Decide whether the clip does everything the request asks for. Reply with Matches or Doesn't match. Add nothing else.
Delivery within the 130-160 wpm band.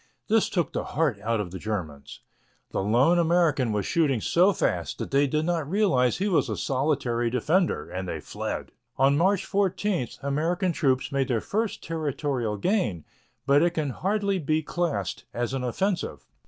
Doesn't match